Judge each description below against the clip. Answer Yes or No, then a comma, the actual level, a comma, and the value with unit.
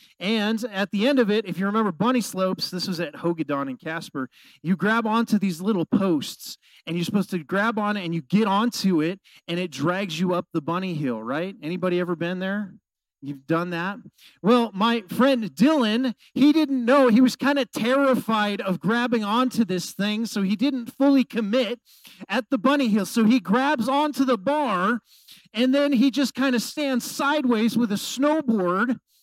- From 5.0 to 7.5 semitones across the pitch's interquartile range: Yes, wide, 5.5 semitones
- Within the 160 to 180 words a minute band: No, average, 190 wpm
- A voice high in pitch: Yes, high, 220 Hz